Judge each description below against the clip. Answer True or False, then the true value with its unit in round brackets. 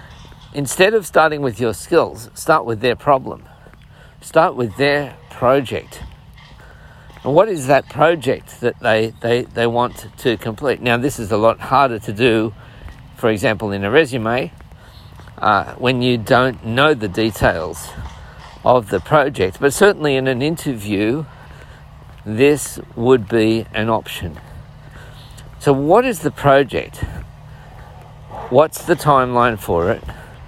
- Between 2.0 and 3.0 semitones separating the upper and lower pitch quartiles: False (3.8 semitones)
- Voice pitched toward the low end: True (125 Hz)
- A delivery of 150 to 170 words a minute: False (135 wpm)